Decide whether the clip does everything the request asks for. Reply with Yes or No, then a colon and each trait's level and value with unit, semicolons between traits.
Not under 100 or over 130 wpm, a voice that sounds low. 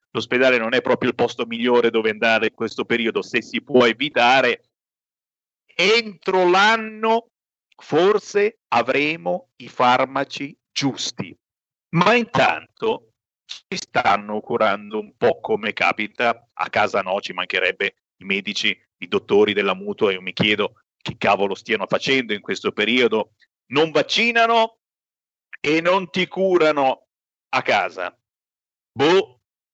No: average, 125 wpm; medium, 150 Hz